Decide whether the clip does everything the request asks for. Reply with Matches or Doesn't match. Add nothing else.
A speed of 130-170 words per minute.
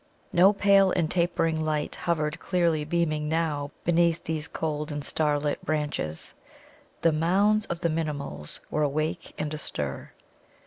Matches